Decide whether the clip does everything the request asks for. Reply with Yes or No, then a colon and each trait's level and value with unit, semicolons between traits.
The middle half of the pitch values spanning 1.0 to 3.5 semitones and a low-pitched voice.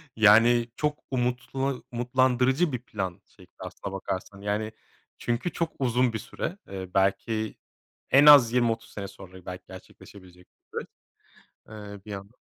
No: average, 4.1 semitones; low, 115 Hz